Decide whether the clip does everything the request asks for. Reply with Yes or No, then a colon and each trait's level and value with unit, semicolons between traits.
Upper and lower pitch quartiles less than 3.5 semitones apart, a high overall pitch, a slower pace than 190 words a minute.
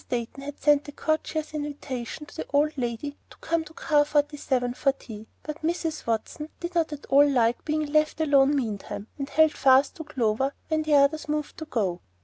No: average, 2.9 semitones; very high, 290 Hz; average, 200 wpm